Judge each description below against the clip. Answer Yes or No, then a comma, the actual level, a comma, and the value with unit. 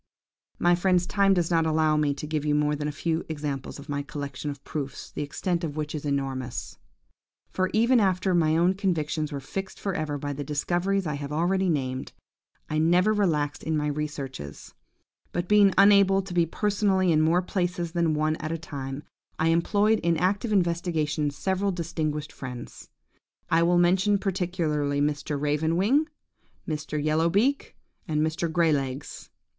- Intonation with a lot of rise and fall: No, average, 3.8 semitones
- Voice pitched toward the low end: No, medium, 160 Hz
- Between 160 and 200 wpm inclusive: Yes, average, 175 wpm